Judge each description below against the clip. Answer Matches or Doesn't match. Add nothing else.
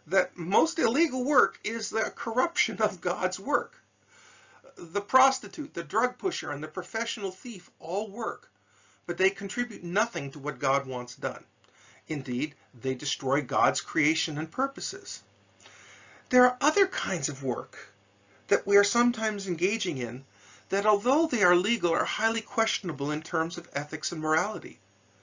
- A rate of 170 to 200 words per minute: Doesn't match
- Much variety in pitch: Matches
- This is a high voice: Doesn't match